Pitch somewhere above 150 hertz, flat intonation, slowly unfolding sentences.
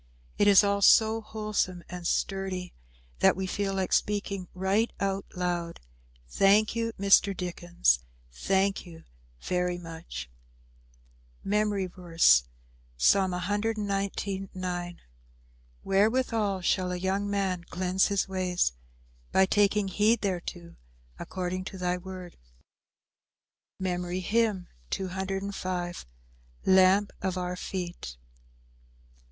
Yes: high, 190 Hz; narrow, 2.0 semitones; slow, 100 wpm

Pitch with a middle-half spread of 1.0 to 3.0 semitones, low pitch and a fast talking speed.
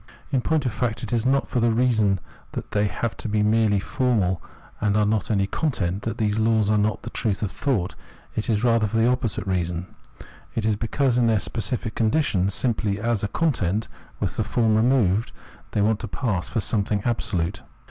Yes: narrow, 2.6 semitones; low, 110 Hz; fast, 210 wpm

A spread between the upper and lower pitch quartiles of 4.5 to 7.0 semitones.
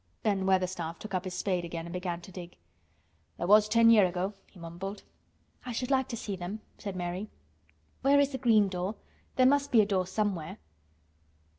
No: average, 3.6 semitones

